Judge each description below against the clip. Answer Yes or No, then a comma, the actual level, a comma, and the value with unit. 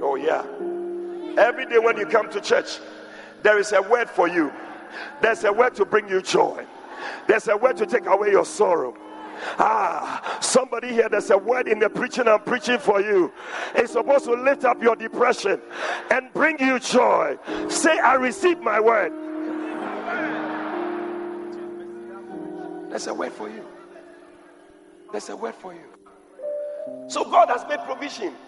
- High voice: Yes, very high, 315 Hz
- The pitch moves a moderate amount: No, wide, 6.4 semitones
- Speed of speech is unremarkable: Yes, average, 155 wpm